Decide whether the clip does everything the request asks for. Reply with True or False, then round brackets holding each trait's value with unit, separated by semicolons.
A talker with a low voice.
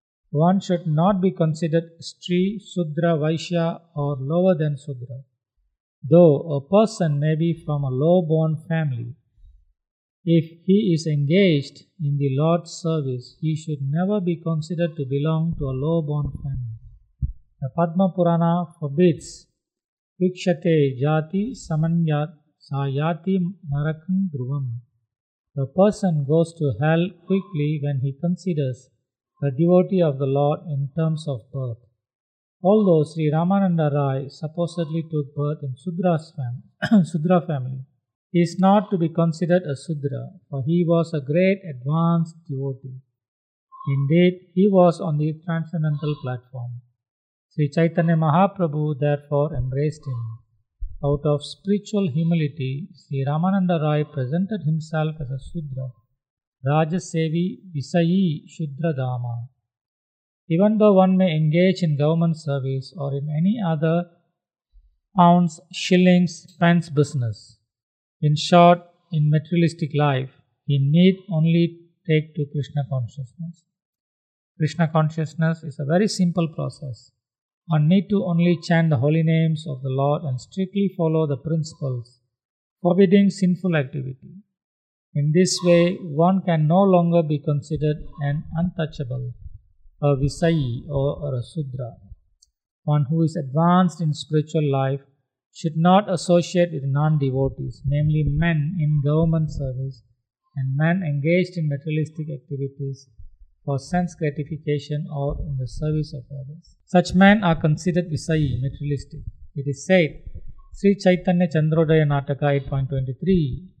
False (155 Hz)